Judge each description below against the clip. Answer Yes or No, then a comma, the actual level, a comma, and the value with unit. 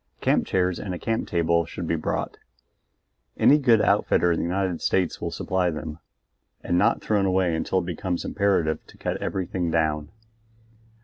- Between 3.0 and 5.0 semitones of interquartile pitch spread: No, narrow, 2.4 semitones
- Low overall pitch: Yes, very low, 90 Hz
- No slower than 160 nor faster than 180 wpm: Yes, average, 170 wpm